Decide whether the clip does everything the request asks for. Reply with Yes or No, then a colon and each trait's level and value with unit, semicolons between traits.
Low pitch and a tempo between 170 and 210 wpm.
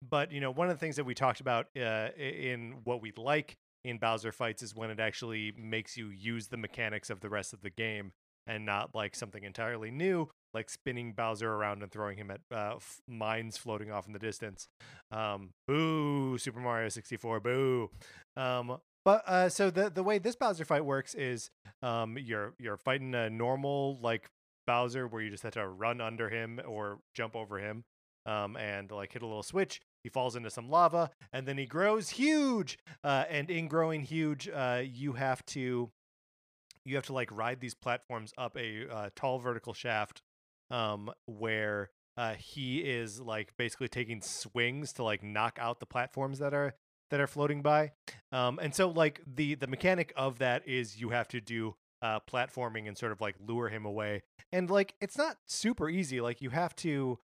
Yes: low, 120 Hz; average, 195 wpm